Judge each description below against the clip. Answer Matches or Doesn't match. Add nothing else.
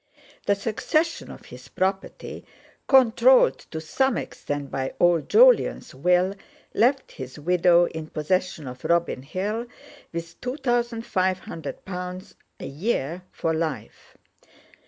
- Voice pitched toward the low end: Doesn't match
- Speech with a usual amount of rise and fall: Doesn't match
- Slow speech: Matches